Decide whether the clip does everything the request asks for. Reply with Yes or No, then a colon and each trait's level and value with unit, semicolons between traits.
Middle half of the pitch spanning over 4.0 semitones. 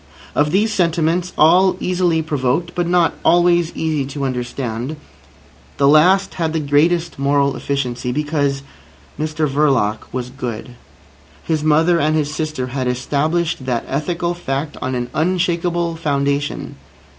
No: average, 3.6 semitones